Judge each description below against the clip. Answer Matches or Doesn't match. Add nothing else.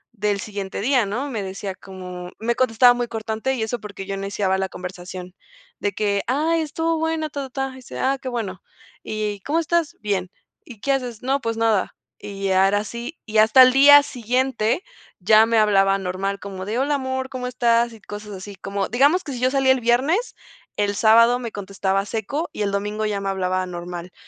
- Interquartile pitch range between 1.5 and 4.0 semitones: Doesn't match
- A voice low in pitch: Doesn't match